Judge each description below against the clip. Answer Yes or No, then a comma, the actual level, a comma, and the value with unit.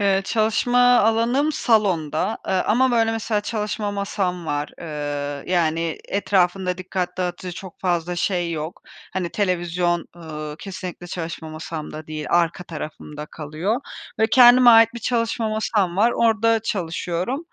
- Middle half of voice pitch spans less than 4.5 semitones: No, average, 4.9 semitones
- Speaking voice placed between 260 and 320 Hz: No, medium, 185 Hz